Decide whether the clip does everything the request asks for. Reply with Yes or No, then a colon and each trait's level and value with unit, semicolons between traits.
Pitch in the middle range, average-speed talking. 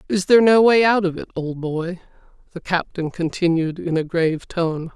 Yes: medium, 175 Hz; average, 195 wpm